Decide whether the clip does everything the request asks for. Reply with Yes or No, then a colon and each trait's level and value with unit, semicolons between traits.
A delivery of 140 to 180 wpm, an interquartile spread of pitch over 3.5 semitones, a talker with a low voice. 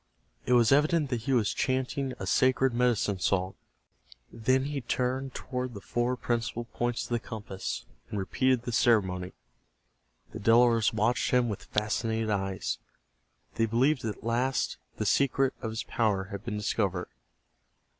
No: average, 155 wpm; average, 3.2 semitones; low, 120 Hz